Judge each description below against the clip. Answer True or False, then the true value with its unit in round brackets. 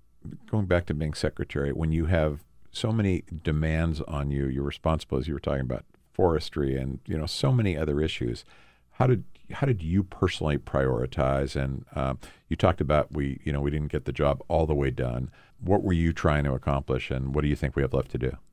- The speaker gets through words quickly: True (220 wpm)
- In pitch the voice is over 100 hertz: False (75 Hz)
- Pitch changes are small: False (3.3 semitones)